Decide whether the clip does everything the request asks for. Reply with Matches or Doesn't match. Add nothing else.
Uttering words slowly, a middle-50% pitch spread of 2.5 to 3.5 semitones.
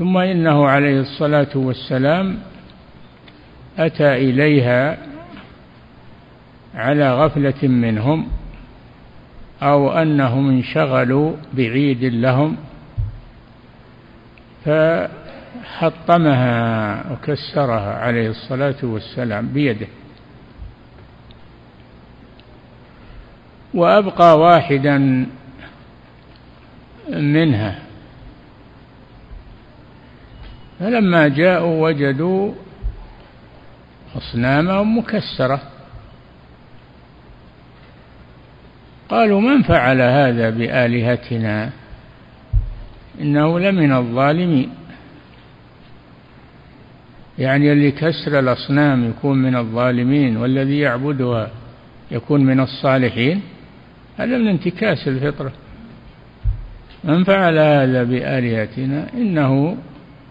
Doesn't match